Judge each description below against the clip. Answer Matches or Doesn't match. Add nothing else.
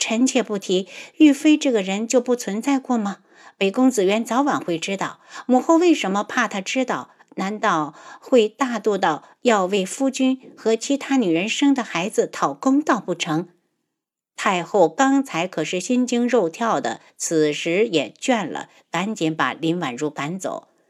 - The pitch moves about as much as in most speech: Doesn't match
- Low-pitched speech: Doesn't match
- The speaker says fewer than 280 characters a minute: Matches